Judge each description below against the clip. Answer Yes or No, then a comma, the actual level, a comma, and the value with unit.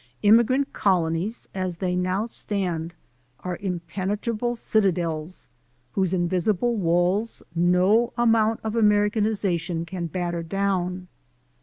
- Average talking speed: No, slow, 105 wpm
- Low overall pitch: No, high, 190 Hz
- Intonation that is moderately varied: Yes, average, 3.5 semitones